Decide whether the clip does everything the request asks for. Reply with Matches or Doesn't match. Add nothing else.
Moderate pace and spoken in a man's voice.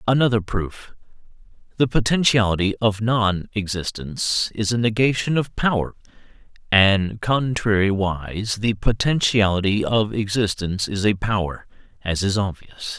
Doesn't match